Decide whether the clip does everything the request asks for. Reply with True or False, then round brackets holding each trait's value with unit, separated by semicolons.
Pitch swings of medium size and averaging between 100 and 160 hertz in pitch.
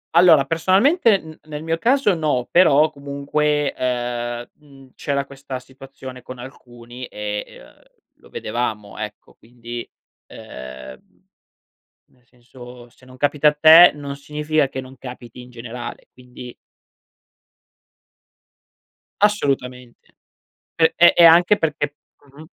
True (4.0 semitones; 135 Hz)